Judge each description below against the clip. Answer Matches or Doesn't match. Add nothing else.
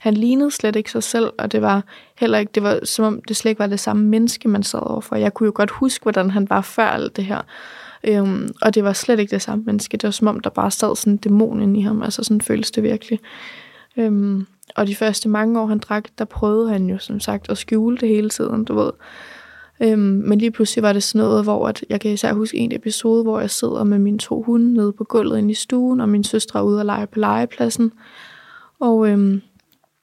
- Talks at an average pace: Doesn't match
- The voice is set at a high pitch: Matches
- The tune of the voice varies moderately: Doesn't match